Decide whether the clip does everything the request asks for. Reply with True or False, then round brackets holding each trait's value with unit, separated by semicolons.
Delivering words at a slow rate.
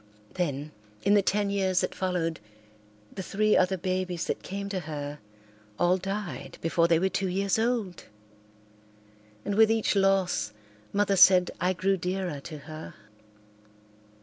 False (145 wpm)